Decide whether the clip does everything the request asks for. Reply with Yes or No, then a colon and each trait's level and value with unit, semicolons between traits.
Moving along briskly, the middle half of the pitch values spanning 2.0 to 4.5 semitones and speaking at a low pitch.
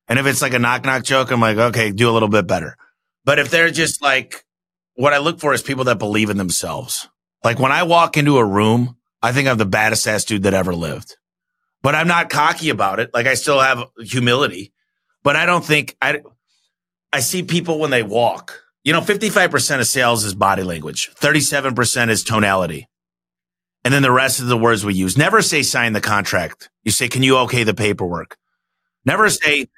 No: fast, 210 wpm; average, 5.0 semitones; low, 125 Hz